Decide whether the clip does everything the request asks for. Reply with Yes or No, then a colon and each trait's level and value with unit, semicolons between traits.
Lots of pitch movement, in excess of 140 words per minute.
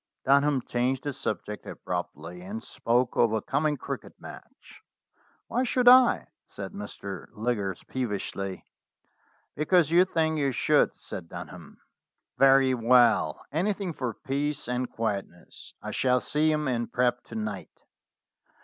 No: wide, 5.8 semitones; slow, 135 wpm